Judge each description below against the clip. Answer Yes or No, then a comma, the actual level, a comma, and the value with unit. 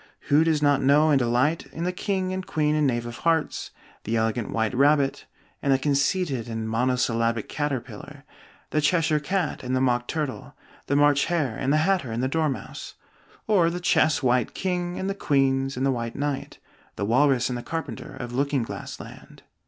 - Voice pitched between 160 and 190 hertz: No, medium, 140 Hz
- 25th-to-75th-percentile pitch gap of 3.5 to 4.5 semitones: Yes, average, 4.2 semitones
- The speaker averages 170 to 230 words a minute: Yes, average, 190 wpm